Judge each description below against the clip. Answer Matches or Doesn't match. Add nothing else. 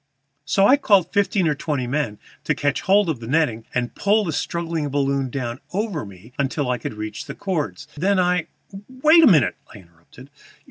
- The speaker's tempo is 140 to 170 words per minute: Doesn't match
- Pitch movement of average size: Doesn't match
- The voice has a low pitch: Doesn't match